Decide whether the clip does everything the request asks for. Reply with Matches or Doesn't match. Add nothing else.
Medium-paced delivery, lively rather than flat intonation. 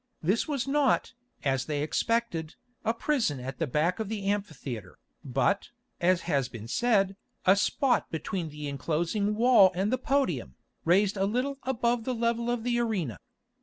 Matches